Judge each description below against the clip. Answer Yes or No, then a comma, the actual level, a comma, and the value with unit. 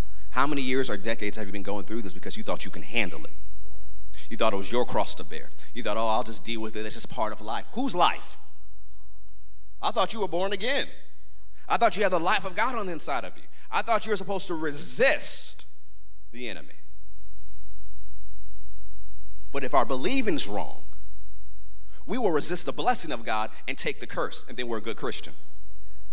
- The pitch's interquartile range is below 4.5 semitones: No, average, 4.8 semitones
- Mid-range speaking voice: No, very low, 90 Hz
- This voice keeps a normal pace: No, fast, 210 wpm